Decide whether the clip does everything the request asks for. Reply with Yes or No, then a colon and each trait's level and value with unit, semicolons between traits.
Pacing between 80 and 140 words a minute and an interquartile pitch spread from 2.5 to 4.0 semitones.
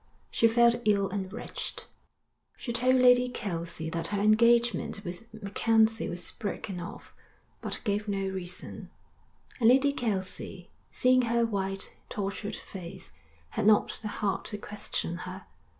Yes: slow, 135 wpm; average, 3.4 semitones